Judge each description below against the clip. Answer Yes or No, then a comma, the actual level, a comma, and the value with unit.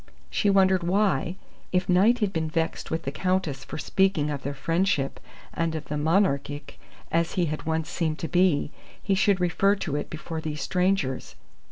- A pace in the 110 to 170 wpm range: No, average, 180 wpm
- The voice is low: No, medium, 165 Hz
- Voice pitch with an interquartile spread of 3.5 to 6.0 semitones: Yes, average, 4.0 semitones